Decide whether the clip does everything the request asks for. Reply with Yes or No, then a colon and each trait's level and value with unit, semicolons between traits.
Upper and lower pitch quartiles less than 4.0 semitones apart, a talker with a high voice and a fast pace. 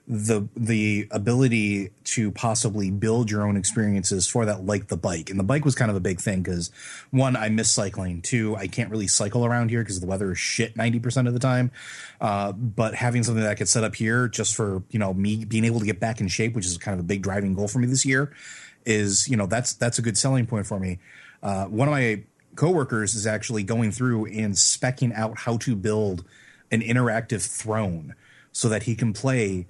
No: average, 2.9 semitones; low, 110 Hz; fast, 225 wpm